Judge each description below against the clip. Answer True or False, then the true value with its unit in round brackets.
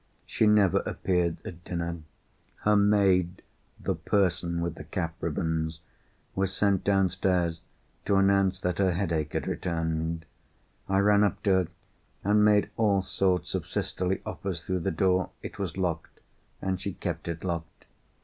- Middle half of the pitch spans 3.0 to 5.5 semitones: False (2.5 semitones)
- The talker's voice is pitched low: True (90 Hz)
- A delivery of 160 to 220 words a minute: False (150 wpm)